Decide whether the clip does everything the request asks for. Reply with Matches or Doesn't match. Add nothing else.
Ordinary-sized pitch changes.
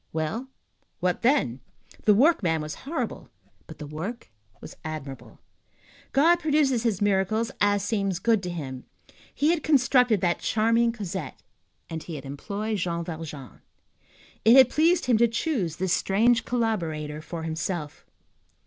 Doesn't match